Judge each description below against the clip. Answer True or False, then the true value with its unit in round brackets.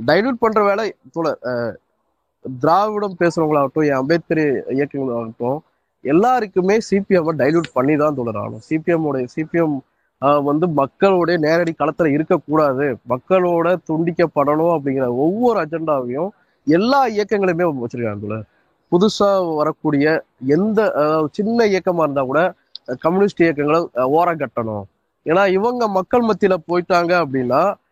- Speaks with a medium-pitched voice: True (160 Hz)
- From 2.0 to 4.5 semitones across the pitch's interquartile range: False (5.0 semitones)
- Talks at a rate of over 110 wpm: False (105 wpm)